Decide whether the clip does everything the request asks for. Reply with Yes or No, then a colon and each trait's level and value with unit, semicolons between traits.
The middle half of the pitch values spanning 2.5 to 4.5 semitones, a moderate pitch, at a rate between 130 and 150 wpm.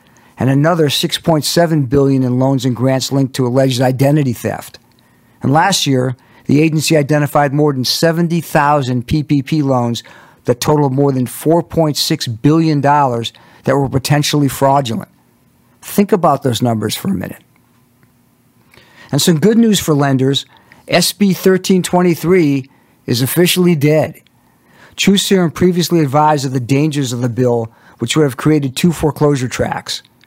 Yes: average, 3.8 semitones; medium, 145 Hz; slow, 135 wpm